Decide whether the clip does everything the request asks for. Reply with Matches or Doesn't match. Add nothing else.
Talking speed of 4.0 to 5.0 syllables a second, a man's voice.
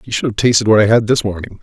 Doesn't match